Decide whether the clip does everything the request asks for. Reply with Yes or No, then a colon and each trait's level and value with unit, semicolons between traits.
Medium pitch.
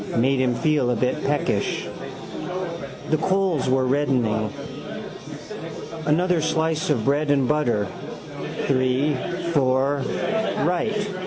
Yes: medium, 145 Hz